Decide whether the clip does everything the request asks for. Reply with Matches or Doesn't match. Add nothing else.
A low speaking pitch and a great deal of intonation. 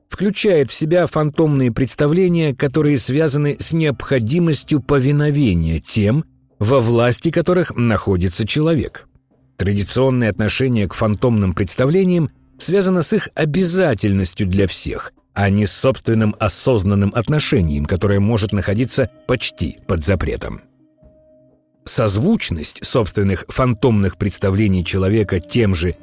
Matches